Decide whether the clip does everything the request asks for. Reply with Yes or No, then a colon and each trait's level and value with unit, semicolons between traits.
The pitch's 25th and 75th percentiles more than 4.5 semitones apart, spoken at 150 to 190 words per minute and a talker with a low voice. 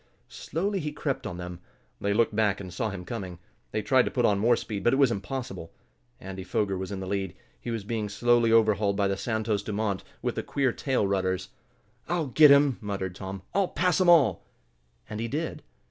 No: average, 5.0 semitones; fast, 205 wpm; low, 110 Hz